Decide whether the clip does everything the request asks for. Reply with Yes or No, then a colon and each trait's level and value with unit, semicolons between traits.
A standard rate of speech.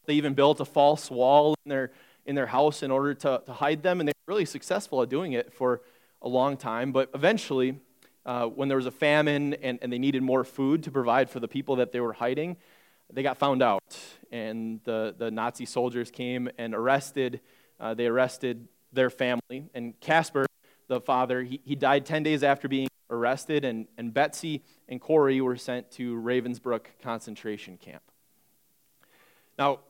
Yes: average, 185 wpm